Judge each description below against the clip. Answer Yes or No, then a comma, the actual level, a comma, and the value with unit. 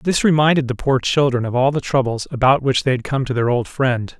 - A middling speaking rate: No, fast, 255 wpm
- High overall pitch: No, low, 130 Hz